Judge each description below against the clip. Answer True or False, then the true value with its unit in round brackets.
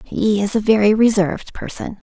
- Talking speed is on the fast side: False (170 wpm)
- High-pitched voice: True (210 Hz)